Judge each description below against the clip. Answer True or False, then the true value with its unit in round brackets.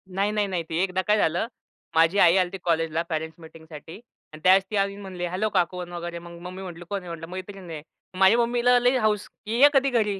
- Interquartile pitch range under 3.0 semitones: False (3.5 semitones)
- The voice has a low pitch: False (185 Hz)